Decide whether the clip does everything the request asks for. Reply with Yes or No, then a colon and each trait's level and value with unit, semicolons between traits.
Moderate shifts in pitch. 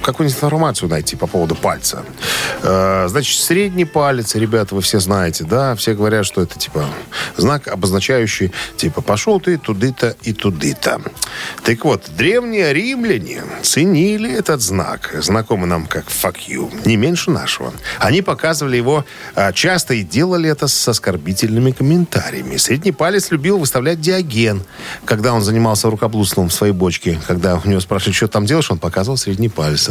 No: wide, 8.5 semitones